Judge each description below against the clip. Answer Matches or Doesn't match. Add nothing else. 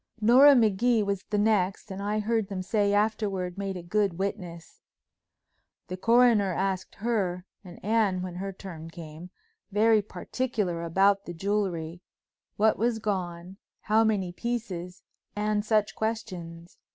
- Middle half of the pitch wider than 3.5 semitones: Doesn't match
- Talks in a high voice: Matches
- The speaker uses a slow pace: Matches